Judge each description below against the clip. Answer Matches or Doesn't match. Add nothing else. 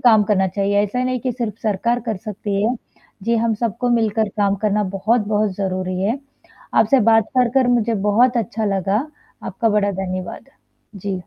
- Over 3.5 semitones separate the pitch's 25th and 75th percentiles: Doesn't match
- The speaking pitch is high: Matches